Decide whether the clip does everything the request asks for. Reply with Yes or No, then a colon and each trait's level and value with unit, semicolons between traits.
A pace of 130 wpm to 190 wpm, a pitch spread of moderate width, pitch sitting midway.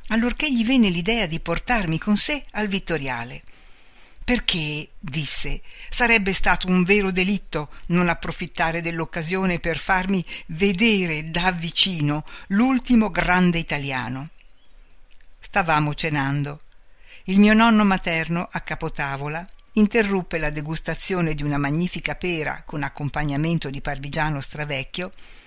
No: slow, 115 wpm; average, 4.6 semitones; medium, 170 Hz